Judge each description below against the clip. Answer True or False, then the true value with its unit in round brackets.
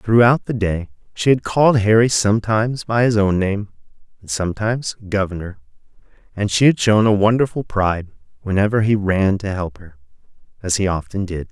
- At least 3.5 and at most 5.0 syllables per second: False (5.5 syllables/s)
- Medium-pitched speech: False (105 Hz)